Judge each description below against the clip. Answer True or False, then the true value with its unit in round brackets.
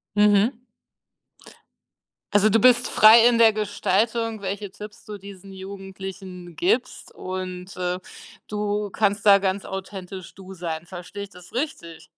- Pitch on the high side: True (200 Hz)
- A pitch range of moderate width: False (2.2 semitones)